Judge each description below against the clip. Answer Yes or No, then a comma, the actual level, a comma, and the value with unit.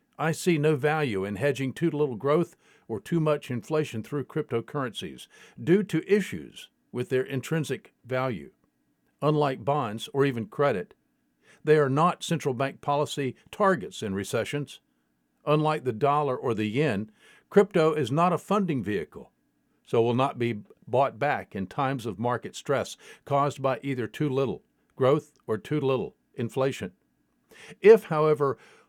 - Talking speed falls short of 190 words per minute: Yes, average, 145 wpm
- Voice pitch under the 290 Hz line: Yes, medium, 140 Hz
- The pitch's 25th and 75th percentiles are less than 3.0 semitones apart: No, average, 3.8 semitones